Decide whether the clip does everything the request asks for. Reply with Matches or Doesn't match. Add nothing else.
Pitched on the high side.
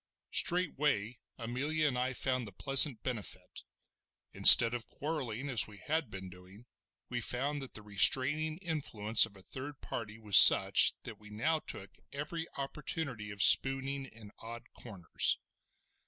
Doesn't match